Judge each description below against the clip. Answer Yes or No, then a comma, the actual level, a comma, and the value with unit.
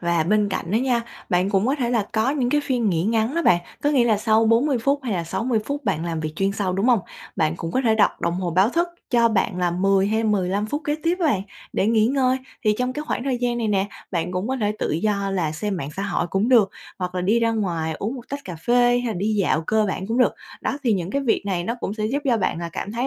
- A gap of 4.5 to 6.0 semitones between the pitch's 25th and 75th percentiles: Yes, average, 4.8 semitones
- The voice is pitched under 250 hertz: Yes, high, 215 Hz